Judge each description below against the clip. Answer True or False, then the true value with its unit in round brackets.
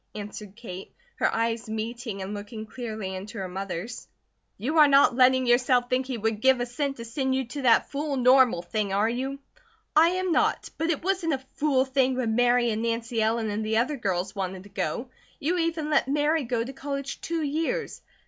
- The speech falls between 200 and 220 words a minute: True (205 wpm)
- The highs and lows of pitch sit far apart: False (4.2 semitones)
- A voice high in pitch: True (245 Hz)